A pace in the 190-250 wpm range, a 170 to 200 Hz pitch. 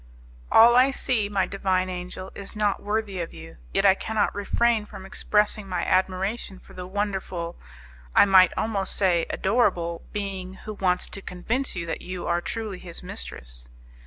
No: average, 165 wpm; high, 190 Hz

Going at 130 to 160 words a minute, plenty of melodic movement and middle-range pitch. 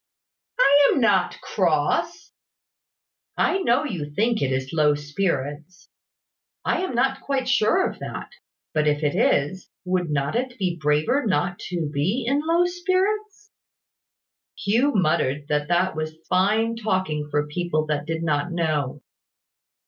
Yes: average, 140 wpm; wide, 8.5 semitones; medium, 180 Hz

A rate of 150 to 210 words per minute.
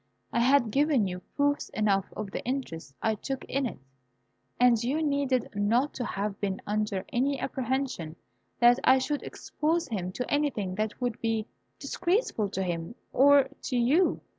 Yes: average, 165 wpm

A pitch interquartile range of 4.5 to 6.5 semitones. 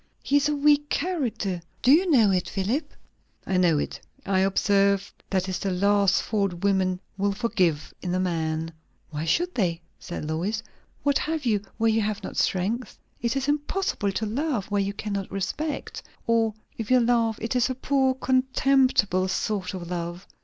Yes: wide, 5.6 semitones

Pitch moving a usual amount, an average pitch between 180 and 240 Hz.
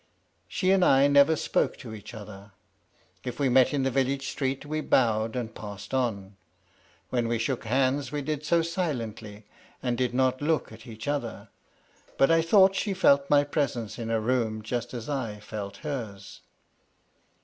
No: average, 4.3 semitones; low, 125 Hz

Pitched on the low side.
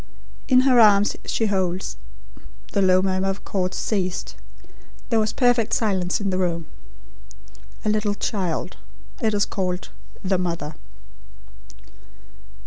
No: high, 195 Hz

